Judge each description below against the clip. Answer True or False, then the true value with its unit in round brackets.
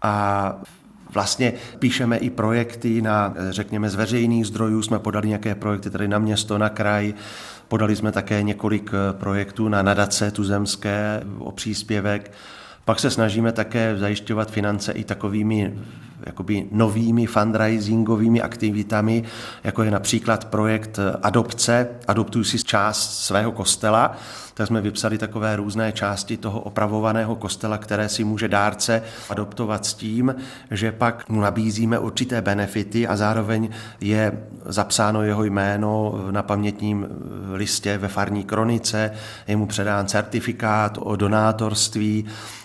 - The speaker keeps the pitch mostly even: True (1.5 semitones)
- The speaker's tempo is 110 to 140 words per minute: True (125 wpm)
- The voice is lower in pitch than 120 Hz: True (105 Hz)